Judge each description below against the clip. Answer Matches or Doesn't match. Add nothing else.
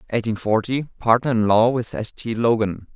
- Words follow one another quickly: Doesn't match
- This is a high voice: Doesn't match